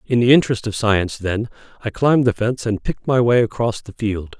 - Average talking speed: No, fast, 230 wpm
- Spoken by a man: Yes, male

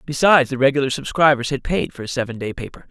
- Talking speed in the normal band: No, fast, 225 wpm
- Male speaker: Yes, male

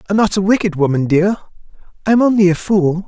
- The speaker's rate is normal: Yes, average, 195 wpm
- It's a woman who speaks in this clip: No, male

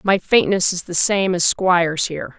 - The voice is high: No, medium, 180 Hz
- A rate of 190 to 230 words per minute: Yes, average, 200 wpm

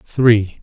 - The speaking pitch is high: No, low, 110 Hz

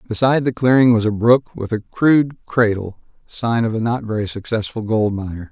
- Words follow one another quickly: No, average, 185 wpm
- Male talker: Yes, male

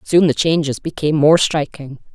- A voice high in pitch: No, medium, 155 Hz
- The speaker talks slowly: No, average, 170 wpm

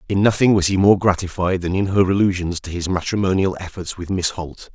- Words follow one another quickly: Yes, fast, 215 wpm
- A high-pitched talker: No, very low, 95 Hz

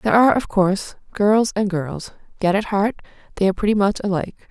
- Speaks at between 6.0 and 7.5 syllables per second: Yes, 6.4 syllables/s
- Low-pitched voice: No, high, 200 Hz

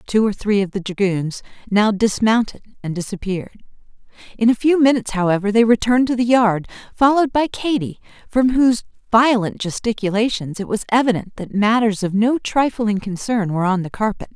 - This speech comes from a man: No, female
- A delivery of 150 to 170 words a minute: Yes, average, 165 wpm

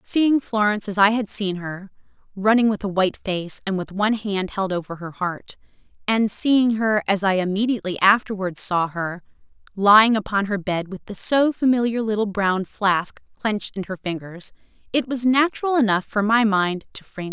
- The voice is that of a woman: Yes, female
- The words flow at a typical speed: Yes, average, 190 wpm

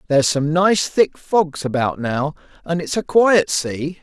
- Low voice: No, medium, 160 Hz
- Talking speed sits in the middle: Yes, average, 180 wpm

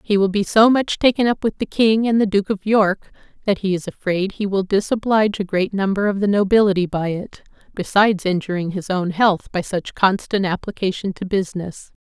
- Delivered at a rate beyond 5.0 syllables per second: Yes, 5.4 syllables/s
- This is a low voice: No, high, 200 Hz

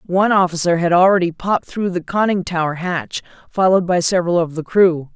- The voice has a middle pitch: Yes, medium, 175 Hz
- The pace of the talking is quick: No, average, 185 wpm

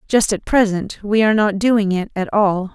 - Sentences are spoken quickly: Yes, fast, 220 wpm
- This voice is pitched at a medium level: No, high, 205 Hz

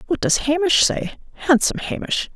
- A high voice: Yes, very high, 330 Hz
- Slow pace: Yes, slow, 125 wpm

